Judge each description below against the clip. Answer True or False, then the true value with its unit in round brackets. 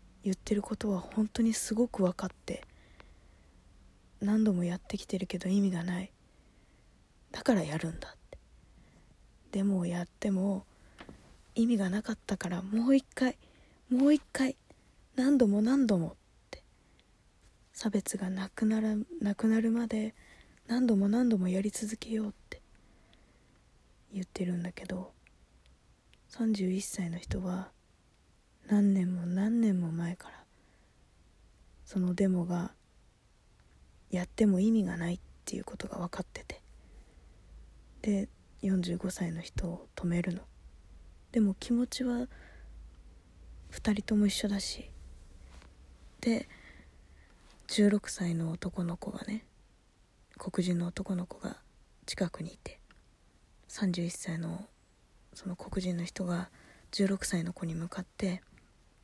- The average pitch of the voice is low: False (185 Hz)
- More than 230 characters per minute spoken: False (210 characters per minute)